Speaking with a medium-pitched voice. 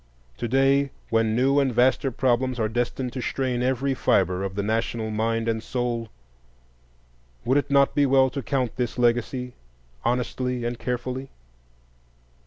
No: low, 125 Hz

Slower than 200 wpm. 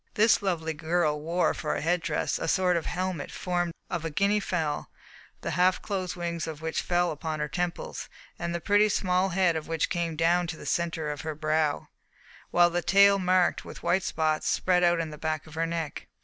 No: fast, 205 wpm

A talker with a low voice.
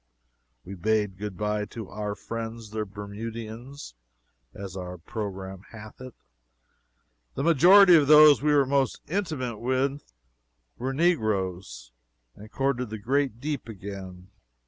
Yes: low, 110 Hz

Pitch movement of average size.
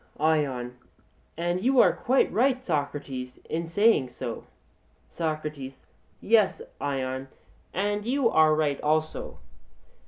No: wide, 6.7 semitones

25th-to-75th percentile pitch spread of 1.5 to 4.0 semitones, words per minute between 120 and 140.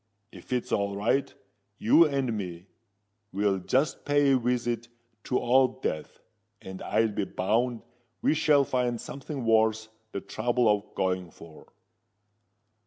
No: average, 4.5 semitones; slow, 135 wpm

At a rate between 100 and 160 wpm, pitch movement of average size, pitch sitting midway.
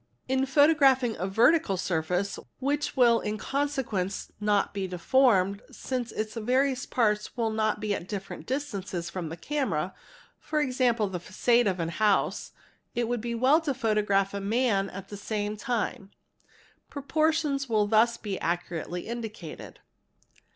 No: average, 145 wpm; average, 4.9 semitones; high, 220 Hz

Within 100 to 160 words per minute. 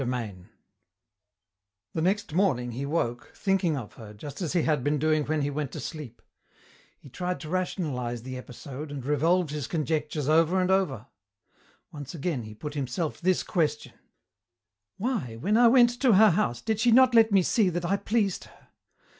No: average, 180 wpm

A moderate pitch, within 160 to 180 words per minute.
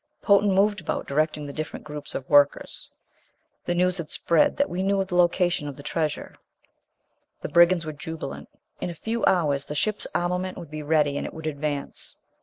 No: medium, 160 Hz; average, 190 wpm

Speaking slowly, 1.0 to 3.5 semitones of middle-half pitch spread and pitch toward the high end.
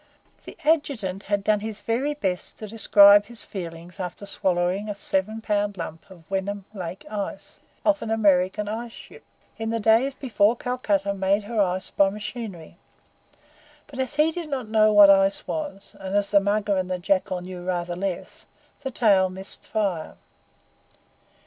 No: average, 165 wpm; average, 2.9 semitones; high, 200 Hz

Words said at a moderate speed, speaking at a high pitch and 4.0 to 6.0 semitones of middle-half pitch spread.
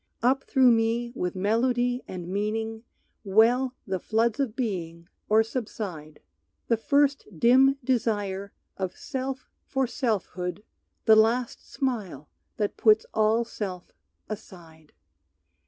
No: slow, 115 wpm; high, 220 Hz; average, 4.3 semitones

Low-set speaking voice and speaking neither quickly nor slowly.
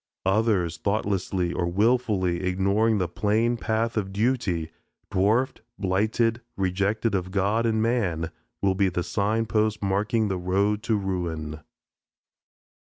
No: low, 100 Hz; slow, 125 wpm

